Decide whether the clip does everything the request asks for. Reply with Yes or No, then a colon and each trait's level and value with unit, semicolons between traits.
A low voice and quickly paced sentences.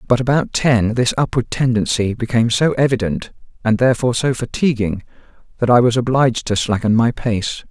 No: low, 120 Hz; average, 165 wpm